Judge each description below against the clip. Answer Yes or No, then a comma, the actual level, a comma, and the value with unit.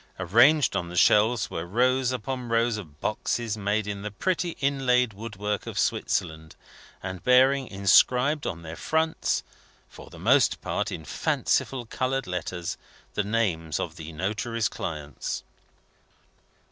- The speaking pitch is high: No, low, 110 Hz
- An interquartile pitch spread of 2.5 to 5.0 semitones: No, wide, 5.6 semitones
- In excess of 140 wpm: No, slow, 135 wpm